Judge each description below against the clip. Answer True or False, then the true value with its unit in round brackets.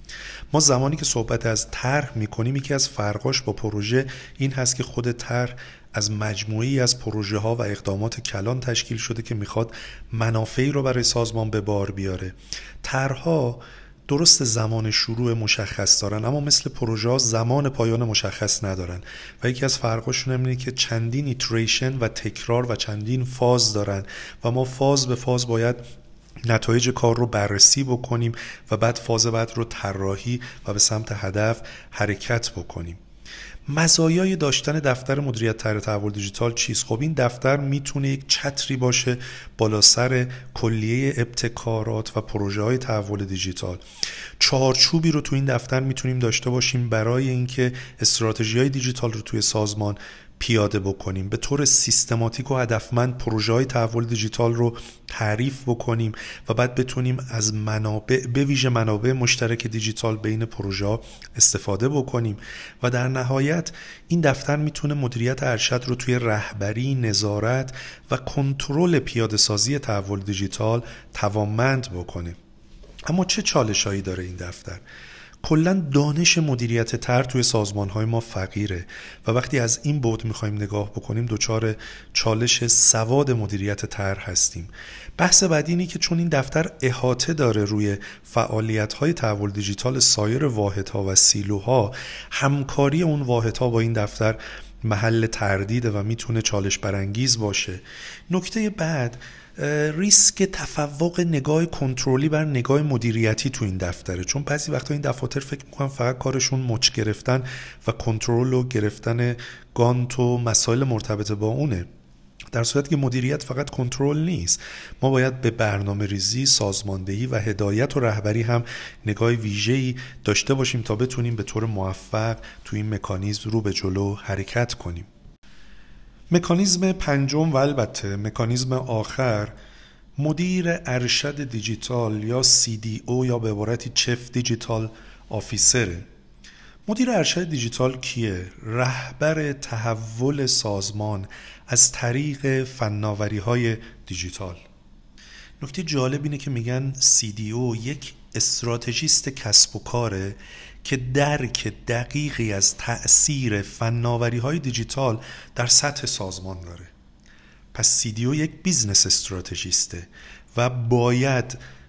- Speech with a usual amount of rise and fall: True (3.6 semitones)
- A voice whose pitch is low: True (120 Hz)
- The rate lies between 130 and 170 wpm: True (135 wpm)